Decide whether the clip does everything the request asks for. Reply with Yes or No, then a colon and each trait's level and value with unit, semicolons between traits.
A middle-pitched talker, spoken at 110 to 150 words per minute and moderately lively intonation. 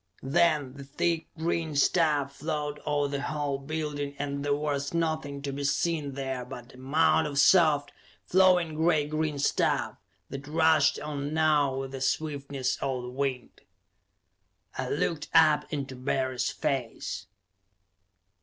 No: medium, 145 Hz; average, 140 wpm; narrow, 2.2 semitones